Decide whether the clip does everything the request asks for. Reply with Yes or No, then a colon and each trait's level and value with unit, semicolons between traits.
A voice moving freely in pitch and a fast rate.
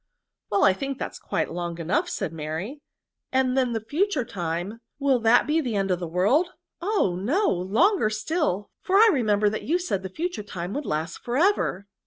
Yes: wide, 8.4 semitones; fast, 215 wpm